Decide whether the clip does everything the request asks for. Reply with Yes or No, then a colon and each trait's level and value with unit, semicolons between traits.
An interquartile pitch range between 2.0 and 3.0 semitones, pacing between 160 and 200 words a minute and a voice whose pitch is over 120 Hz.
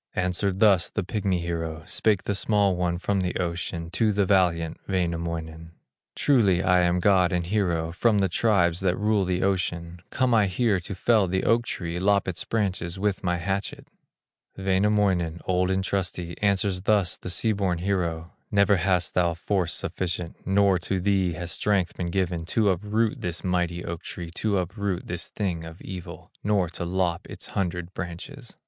No: narrow, 2.6 semitones; average, 175 wpm; very low, 90 Hz